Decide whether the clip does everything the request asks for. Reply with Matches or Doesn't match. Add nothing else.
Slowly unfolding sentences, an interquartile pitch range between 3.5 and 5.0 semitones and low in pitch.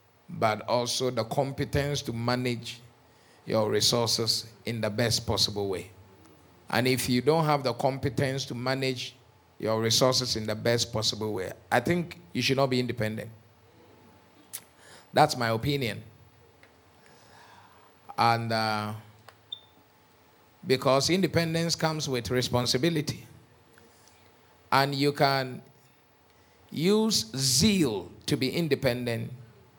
Matches